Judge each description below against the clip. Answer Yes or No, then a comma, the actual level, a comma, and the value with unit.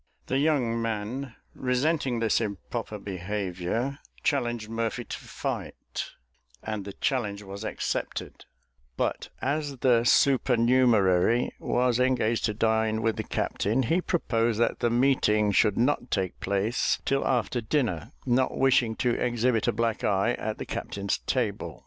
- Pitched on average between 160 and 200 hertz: No, low, 115 Hz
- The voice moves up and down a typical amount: Yes, average, 3.2 semitones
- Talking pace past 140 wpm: No, slow, 135 wpm